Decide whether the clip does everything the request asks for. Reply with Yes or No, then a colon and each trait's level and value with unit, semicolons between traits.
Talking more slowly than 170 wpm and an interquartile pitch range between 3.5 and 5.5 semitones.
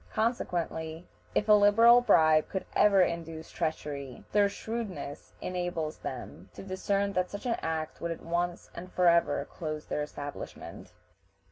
Yes: average, 140 wpm; average, 4.1 semitones